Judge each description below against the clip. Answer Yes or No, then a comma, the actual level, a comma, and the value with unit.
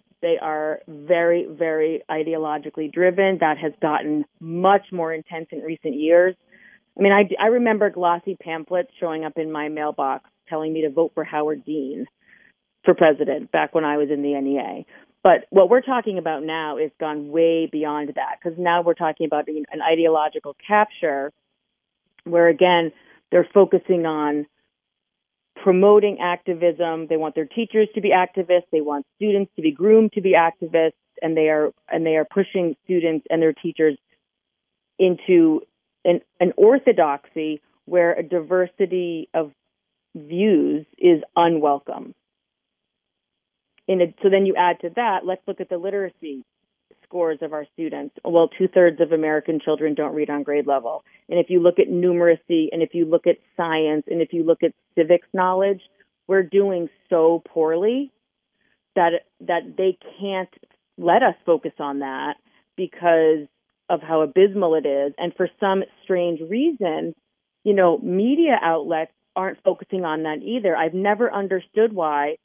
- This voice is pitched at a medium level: Yes, medium, 170 Hz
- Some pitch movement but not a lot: Yes, average, 3.3 semitones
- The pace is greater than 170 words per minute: No, average, 160 wpm